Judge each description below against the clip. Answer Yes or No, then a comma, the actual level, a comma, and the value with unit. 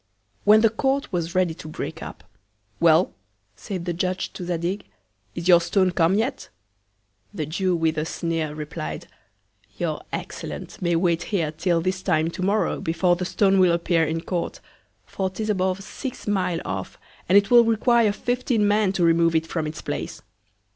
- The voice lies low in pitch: No, medium, 180 Hz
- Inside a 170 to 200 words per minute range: Yes, average, 175 wpm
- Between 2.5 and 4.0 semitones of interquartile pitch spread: Yes, average, 3.4 semitones